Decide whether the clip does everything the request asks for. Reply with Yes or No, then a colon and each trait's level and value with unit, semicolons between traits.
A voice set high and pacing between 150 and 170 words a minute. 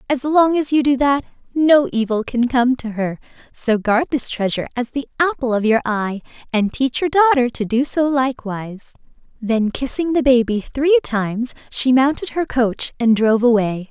No: very high, 250 Hz; average, 185 wpm